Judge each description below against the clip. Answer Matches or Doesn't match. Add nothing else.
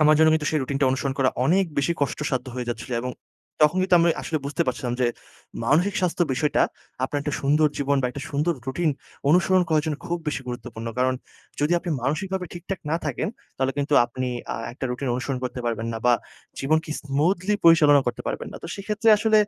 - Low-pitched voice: Doesn't match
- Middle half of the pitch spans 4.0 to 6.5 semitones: Matches